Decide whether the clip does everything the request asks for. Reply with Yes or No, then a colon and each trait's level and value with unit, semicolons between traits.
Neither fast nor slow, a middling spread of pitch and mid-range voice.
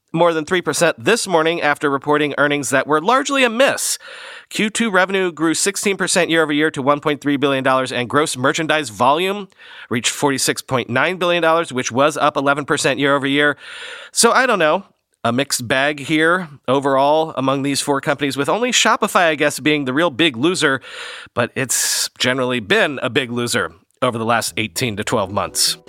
Yes: average, 170 wpm; average, 3.8 semitones; medium, 150 Hz